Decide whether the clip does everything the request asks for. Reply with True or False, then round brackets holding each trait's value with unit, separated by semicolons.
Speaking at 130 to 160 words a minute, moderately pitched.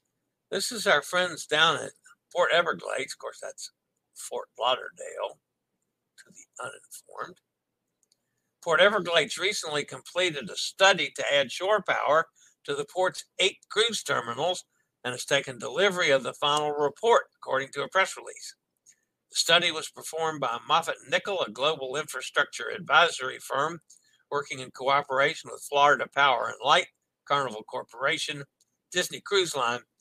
True (140 wpm; 180 Hz)